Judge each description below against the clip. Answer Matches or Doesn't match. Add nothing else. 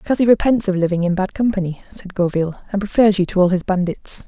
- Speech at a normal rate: Doesn't match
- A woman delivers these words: Matches